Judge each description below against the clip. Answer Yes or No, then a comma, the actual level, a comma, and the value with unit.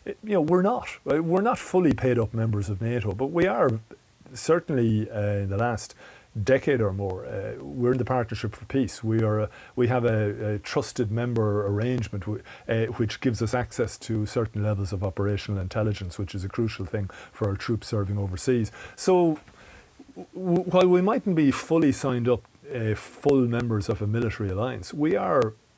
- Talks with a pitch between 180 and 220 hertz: No, low, 115 Hz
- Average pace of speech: Yes, average, 185 wpm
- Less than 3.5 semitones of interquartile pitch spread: No, average, 3.8 semitones